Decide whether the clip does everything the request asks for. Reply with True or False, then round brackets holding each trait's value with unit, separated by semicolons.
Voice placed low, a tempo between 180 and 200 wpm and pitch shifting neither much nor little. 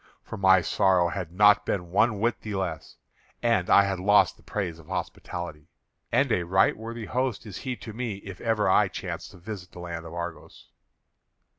True (95 Hz; 190 wpm; 3.6 semitones)